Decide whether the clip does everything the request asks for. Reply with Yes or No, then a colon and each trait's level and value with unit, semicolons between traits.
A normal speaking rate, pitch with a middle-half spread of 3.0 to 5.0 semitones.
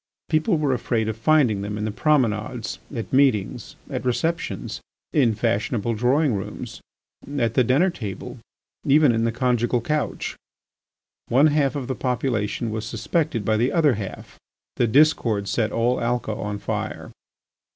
Yes: average, 150 wpm; average, 4.3 semitones